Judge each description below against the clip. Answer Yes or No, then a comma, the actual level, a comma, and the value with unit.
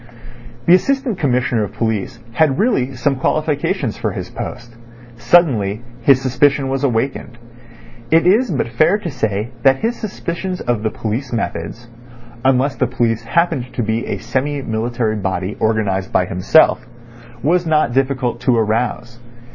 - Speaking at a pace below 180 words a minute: Yes, average, 145 wpm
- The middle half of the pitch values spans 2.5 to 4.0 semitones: No, average, 4.4 semitones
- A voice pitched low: Yes, low, 125 Hz